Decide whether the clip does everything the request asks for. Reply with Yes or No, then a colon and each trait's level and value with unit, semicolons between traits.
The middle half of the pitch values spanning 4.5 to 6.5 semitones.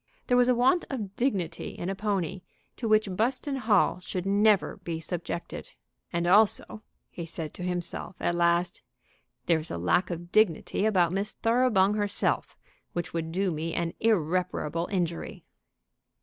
No: average, 3.9 semitones